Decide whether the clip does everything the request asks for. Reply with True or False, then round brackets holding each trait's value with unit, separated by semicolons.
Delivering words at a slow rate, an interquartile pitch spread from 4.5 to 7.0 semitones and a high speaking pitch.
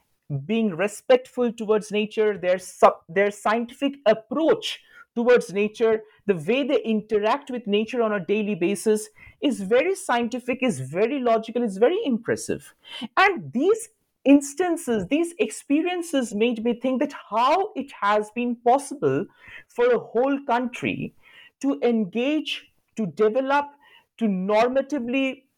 True (125 wpm; 4.8 semitones; 240 Hz)